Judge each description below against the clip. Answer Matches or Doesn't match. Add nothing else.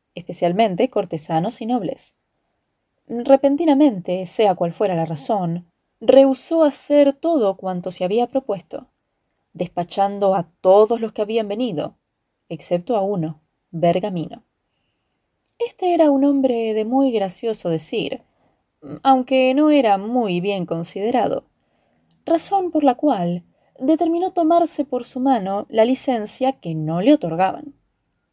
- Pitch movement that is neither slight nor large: Doesn't match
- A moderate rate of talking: Doesn't match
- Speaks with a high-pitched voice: Matches